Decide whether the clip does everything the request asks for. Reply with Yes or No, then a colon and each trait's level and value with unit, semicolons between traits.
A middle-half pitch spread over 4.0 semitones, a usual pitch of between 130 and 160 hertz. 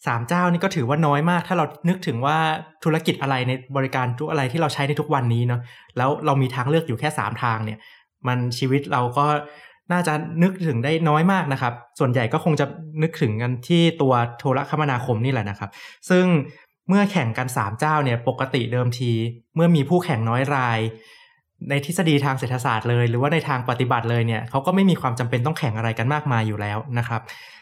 Yes: average, 4.4 semitones; medium, 140 Hz